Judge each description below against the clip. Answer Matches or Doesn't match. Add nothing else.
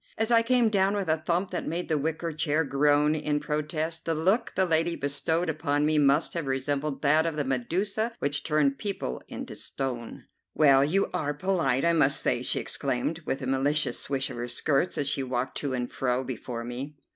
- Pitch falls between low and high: Matches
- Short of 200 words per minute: Doesn't match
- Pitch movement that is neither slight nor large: Matches